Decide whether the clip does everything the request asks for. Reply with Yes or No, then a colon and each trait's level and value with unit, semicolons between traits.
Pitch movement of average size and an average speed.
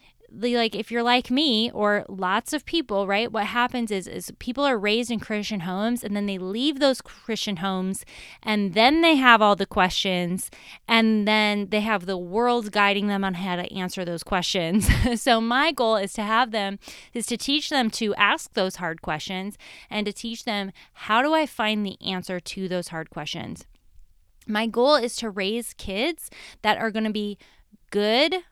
Yes: average, 3.3 semitones; average, 190 wpm